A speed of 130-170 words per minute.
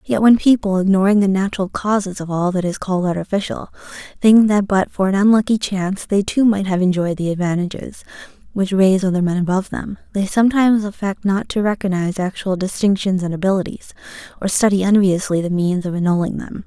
No: average, 185 wpm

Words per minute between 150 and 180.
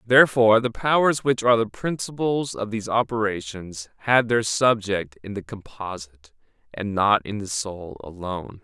Yes: average, 155 wpm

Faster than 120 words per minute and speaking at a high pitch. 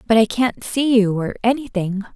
Yes: average, 140 wpm; high, 220 Hz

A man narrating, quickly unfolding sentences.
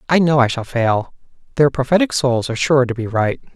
Yes: male; fast, 220 wpm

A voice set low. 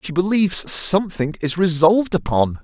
No: medium, 175 Hz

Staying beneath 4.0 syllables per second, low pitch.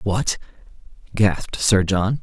Yes: 3.7 syllables/s; low, 105 Hz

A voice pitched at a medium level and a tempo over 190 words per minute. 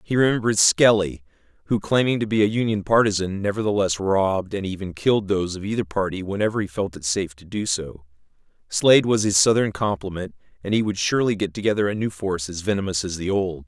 No: low, 100 Hz; average, 200 wpm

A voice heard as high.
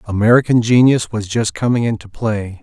No: low, 110 Hz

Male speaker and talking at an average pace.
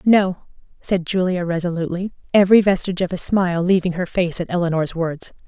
No: female; average, 165 wpm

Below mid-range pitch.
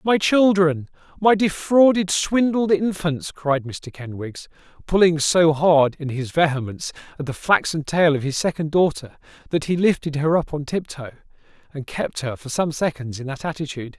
No: medium, 160 Hz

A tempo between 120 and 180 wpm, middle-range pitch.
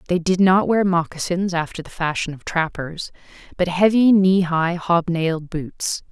Yes: average, 155 wpm; medium, 175 Hz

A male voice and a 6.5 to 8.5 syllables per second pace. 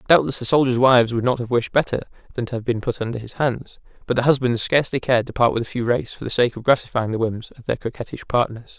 Yes: male; 6.7 syllables/s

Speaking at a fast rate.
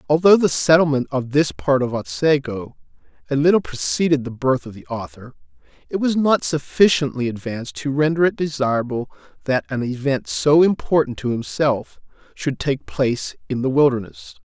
No: average, 160 wpm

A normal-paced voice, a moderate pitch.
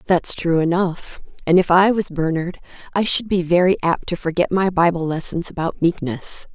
Yes: average, 185 wpm; medium, 175 Hz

